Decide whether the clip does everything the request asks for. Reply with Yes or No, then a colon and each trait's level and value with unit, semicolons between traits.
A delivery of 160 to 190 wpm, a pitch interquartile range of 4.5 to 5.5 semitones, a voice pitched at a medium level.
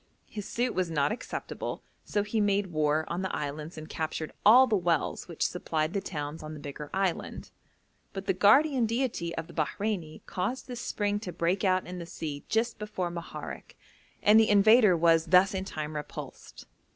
Yes: average, 185 wpm; average, 4.8 semitones; medium, 180 Hz